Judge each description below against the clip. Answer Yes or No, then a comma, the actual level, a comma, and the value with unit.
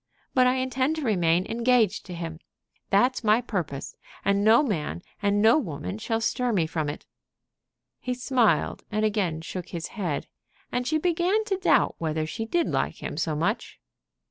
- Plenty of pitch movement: Yes, wide, 6.8 semitones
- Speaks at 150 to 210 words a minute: Yes, average, 170 wpm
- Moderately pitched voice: No, high, 215 Hz